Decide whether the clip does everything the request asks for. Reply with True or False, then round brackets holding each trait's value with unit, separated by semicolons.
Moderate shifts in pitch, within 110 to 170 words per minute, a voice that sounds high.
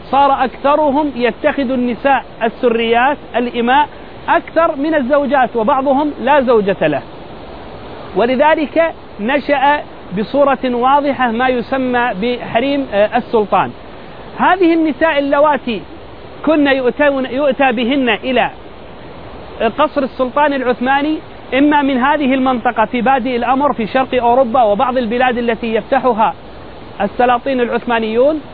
False (3.0 semitones; 100 wpm; 265 Hz)